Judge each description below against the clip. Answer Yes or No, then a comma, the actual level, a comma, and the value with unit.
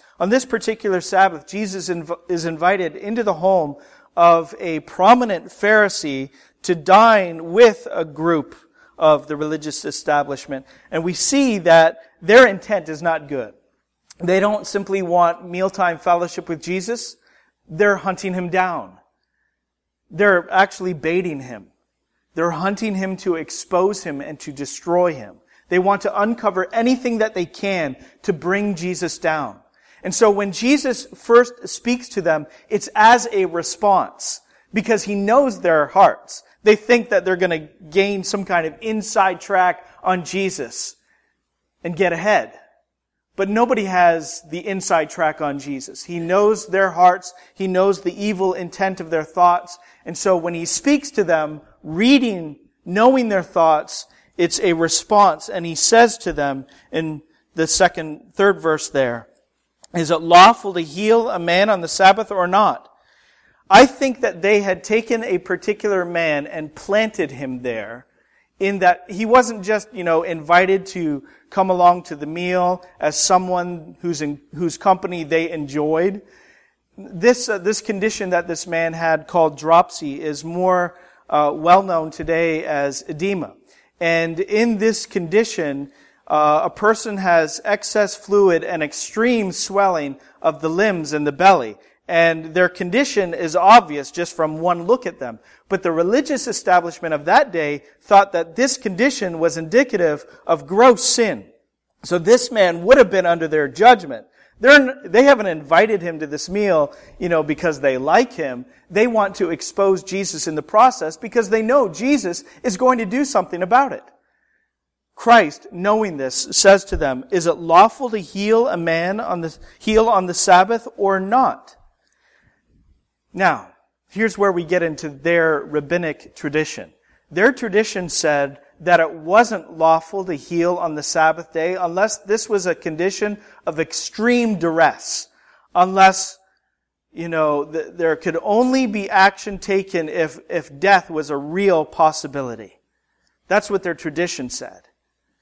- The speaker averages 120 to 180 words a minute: Yes, average, 155 wpm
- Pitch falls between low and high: Yes, medium, 180 Hz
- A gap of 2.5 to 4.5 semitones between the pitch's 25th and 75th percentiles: Yes, average, 4.1 semitones